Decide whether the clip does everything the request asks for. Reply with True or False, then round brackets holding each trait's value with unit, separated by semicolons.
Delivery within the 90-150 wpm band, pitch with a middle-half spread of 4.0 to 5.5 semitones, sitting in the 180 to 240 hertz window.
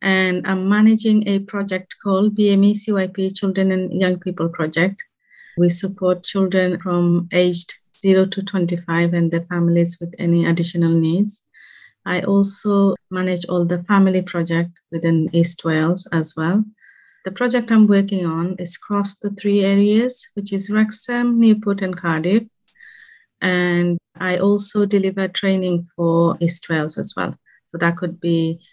False (145 wpm; 2.7 semitones; 185 Hz)